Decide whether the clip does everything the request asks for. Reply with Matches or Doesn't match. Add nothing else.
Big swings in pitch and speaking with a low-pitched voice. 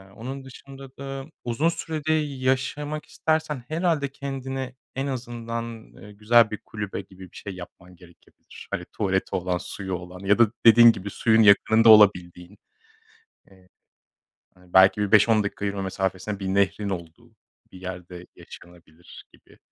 Matches